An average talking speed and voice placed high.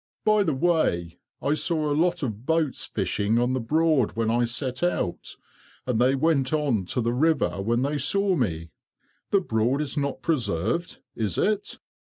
No: average, 170 wpm; low, 135 Hz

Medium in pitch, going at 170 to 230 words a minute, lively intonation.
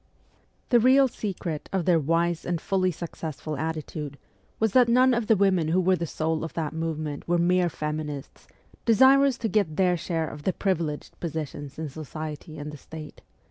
No: medium, 165 Hz; average, 180 wpm; average, 3.7 semitones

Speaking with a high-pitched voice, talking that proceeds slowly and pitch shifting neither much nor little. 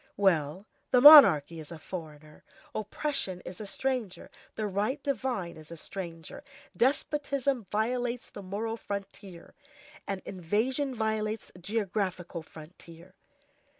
No: high, 200 Hz; slow, 115 wpm; wide, 5.9 semitones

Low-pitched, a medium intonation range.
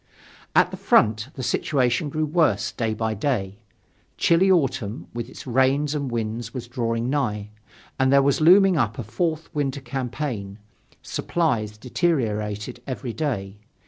Yes: low, 125 Hz; average, 4.9 semitones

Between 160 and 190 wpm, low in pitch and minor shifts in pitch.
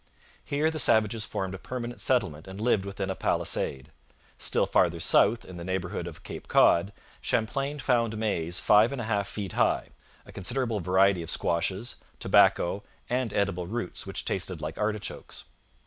No: average, 165 wpm; low, 100 Hz; average, 4.1 semitones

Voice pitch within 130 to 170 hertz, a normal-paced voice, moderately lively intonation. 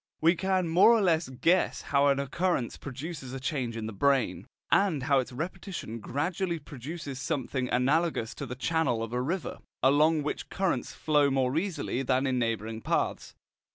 Yes: medium, 140 Hz; average, 170 wpm; average, 4.7 semitones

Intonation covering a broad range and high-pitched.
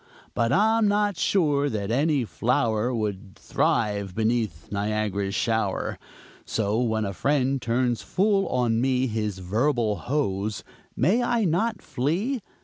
No: wide, 6.0 semitones; low, 120 Hz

